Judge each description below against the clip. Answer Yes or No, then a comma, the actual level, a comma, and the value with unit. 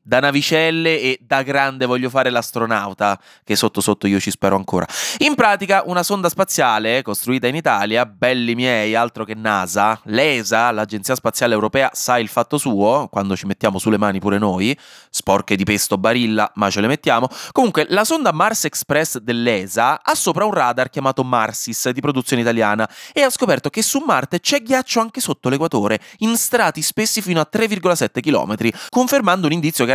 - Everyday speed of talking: No, fast, 175 wpm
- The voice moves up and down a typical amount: No, wide, 7.3 semitones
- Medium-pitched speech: No, low, 125 Hz